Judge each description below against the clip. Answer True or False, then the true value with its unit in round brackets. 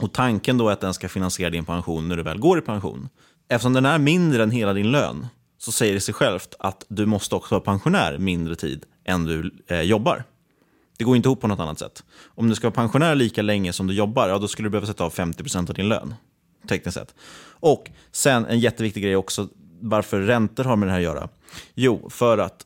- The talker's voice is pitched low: True (105 Hz)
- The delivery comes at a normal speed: False (235 wpm)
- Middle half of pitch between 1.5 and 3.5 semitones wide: False (4.2 semitones)